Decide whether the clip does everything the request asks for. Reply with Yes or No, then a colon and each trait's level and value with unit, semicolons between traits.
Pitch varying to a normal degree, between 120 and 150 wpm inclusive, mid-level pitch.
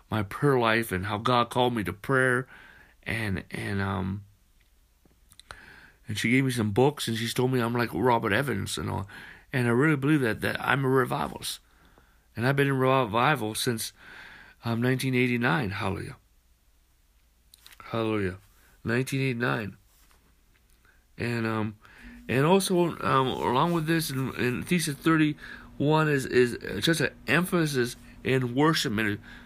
No: average, 4.6 semitones; average, 140 wpm; low, 120 Hz